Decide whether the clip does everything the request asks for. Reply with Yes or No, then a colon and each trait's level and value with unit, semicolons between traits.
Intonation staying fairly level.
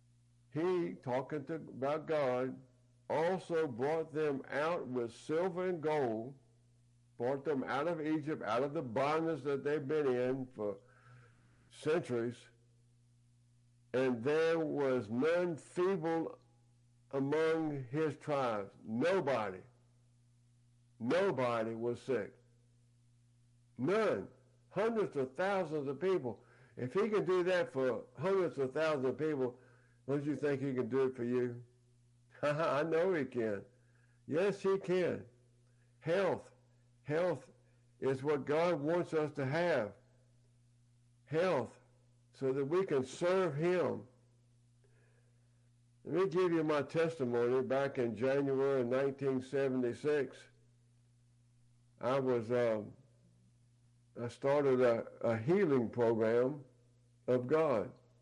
No: average, 4.1 semitones